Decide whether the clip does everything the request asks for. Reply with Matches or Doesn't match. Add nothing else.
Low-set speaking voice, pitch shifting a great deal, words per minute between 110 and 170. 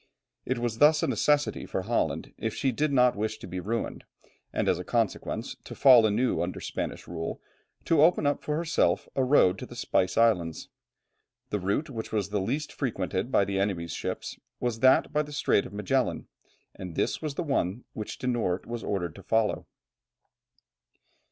Doesn't match